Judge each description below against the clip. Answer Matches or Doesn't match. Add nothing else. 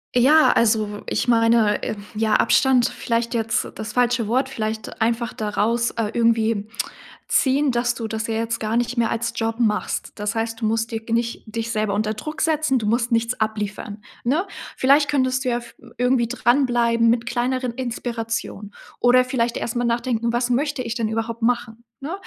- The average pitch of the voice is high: Matches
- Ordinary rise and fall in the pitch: Doesn't match